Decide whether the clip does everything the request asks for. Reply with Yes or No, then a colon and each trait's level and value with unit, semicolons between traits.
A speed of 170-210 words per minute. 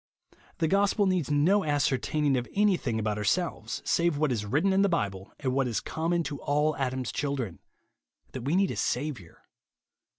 Yes: average, 175 wpm